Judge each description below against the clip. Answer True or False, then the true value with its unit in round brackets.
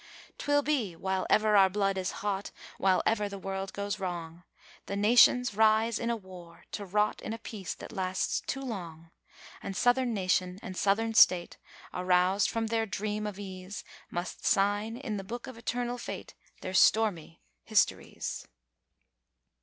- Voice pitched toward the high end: True (200 Hz)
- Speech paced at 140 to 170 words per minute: True (160 wpm)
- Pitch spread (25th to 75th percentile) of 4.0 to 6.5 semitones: False (3.2 semitones)